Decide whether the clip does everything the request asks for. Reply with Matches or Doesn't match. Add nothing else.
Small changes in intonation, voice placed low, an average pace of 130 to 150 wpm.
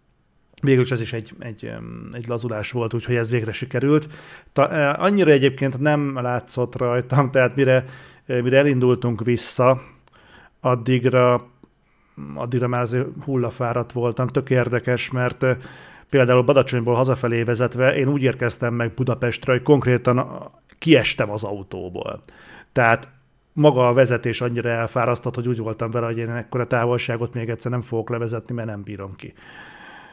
Matches